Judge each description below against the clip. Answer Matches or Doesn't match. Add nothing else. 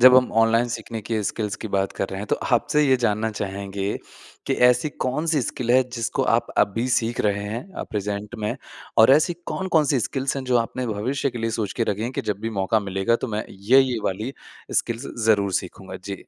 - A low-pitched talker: Matches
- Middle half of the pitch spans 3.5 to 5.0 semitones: Matches